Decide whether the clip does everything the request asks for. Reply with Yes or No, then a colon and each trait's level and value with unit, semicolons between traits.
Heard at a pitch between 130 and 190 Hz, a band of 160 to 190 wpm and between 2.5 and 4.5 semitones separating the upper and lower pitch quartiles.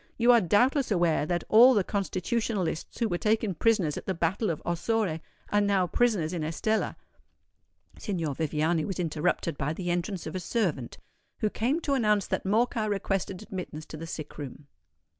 No: medium, 185 Hz; average, 175 wpm; average, 4.9 semitones